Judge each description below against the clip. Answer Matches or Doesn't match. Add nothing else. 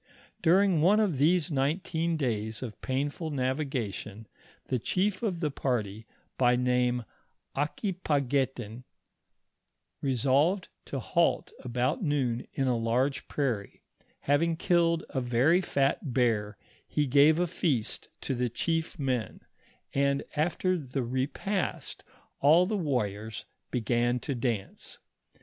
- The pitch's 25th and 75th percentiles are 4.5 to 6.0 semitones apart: Matches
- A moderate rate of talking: Doesn't match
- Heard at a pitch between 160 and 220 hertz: Doesn't match